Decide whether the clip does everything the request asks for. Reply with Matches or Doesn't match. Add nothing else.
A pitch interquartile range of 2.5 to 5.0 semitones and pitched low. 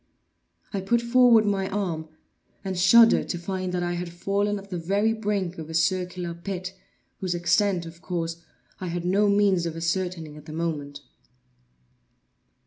Doesn't match